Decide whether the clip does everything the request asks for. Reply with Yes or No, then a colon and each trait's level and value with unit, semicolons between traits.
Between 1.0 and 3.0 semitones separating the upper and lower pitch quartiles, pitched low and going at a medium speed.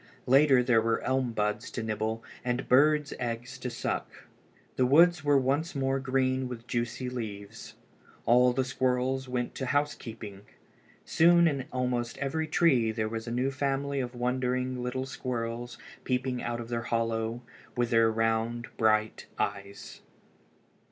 Yes: narrow, 2.5 semitones; low, 125 Hz; average, 145 wpm